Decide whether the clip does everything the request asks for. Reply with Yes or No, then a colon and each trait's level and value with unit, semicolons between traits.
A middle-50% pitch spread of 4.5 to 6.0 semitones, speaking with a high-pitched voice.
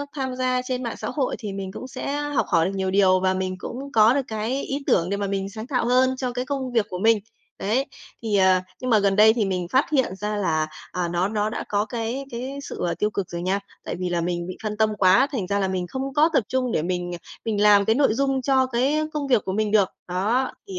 Yes: average, 5.2 semitones; high, 215 Hz